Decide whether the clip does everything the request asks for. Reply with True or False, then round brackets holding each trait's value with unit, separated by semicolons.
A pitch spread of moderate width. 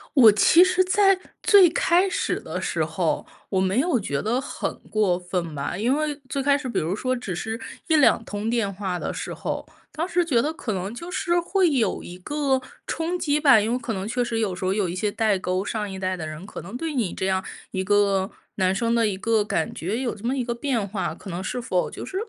False (6.9 semitones)